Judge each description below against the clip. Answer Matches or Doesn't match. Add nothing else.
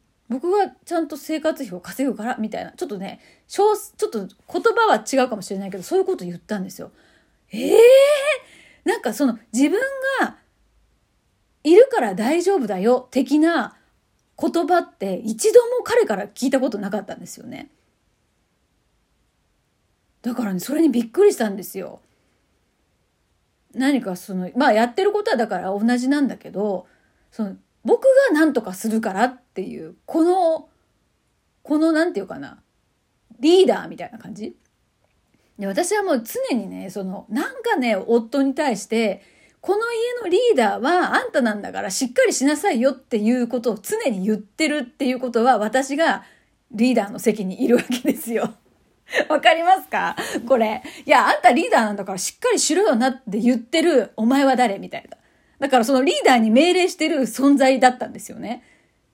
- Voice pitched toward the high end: Matches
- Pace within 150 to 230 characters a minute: Doesn't match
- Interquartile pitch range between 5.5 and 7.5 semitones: Matches